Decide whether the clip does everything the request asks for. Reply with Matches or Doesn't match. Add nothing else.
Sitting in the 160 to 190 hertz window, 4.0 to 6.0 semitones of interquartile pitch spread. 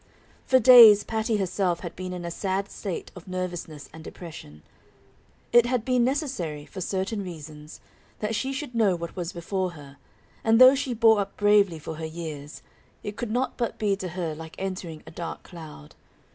Matches